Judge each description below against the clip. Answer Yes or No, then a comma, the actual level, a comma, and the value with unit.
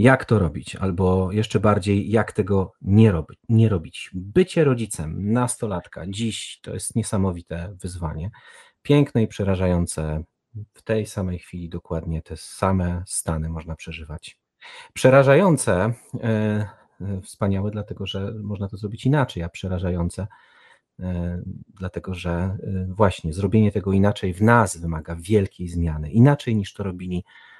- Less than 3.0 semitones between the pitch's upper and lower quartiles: No, average, 3.8 semitones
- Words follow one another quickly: No, average, 130 wpm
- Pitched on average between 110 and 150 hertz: No, low, 100 Hz